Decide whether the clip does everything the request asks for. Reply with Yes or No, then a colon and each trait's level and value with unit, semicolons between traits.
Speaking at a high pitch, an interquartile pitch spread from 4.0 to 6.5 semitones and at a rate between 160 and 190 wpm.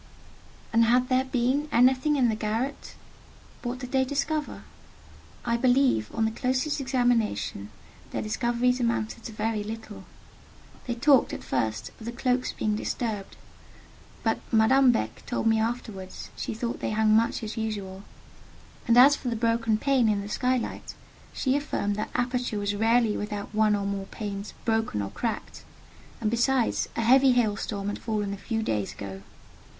No: high, 230 Hz; average, 3.1 semitones; average, 165 wpm